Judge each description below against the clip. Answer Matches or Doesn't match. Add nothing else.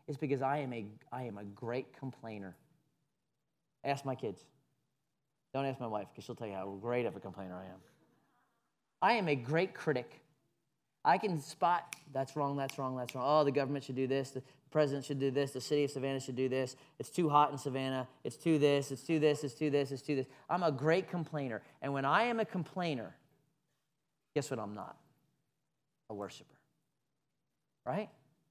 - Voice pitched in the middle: Matches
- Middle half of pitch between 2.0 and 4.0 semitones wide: Matches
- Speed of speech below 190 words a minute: Doesn't match